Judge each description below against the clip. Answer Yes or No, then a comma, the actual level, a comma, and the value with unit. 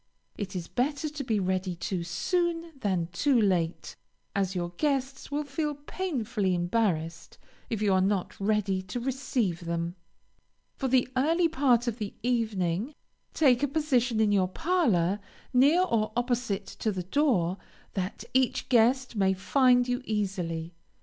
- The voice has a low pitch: No, high, 220 Hz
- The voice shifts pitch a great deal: Yes, wide, 6.1 semitones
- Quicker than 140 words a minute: Yes, average, 150 wpm